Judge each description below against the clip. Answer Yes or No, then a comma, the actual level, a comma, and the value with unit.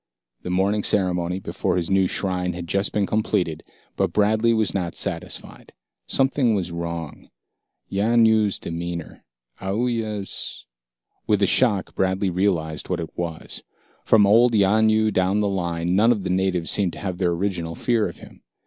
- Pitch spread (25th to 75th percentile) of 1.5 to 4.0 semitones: Yes, average, 3.4 semitones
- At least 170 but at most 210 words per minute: No, average, 155 wpm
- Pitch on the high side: No, very low, 95 Hz